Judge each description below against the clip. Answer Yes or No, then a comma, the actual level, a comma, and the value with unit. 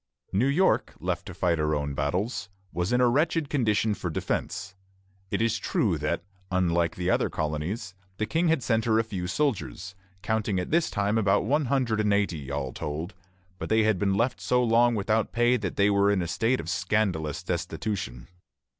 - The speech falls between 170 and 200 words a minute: Yes, average, 190 wpm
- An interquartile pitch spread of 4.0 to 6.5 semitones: Yes, average, 4.7 semitones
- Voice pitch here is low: Yes, low, 105 Hz